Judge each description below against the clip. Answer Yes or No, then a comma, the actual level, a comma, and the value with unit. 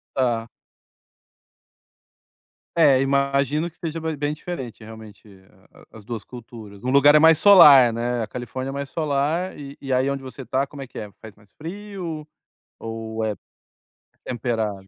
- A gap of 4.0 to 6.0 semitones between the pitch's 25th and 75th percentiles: Yes, average, 4.9 semitones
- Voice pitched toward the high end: No, low, 135 Hz